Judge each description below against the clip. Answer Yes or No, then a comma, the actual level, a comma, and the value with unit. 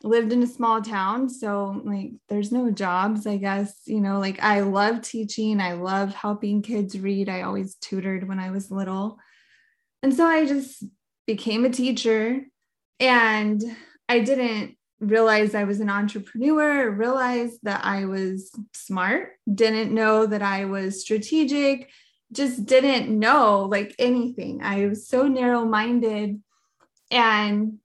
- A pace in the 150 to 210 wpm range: No, average, 140 wpm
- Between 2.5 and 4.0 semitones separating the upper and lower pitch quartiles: Yes, average, 3.3 semitones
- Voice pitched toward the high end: Yes, high, 215 Hz